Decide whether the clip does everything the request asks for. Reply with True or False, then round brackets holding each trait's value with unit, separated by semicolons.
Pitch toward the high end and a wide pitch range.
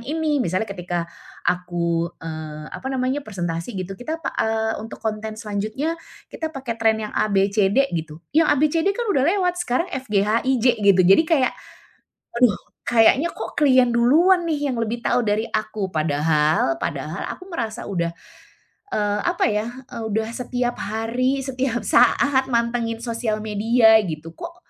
False (230 Hz; 4.7 semitones)